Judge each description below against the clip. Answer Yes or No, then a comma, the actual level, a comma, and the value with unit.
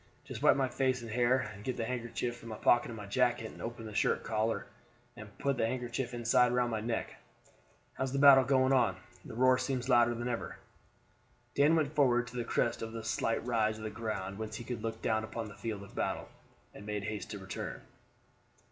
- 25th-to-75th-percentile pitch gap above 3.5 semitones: No, narrow, 2.4 semitones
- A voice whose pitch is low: Yes, low, 120 Hz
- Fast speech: Yes, fast, 220 wpm